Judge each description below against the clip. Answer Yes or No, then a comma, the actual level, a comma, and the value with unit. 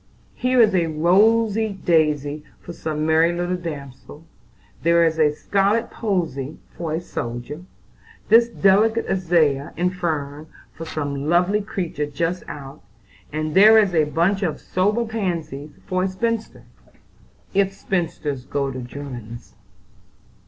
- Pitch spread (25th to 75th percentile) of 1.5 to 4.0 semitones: No, average, 4.7 semitones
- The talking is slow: Yes, slow, 130 wpm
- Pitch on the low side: No, medium, 170 Hz